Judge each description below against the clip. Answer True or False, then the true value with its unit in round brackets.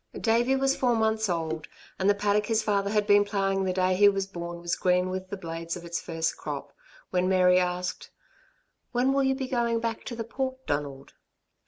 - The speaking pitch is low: False (195 Hz)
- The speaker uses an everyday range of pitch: True (4.1 semitones)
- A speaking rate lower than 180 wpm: False (205 wpm)